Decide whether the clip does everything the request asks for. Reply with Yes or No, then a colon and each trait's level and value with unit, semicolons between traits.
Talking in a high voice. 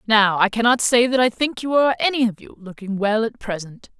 Yes: high, 225 Hz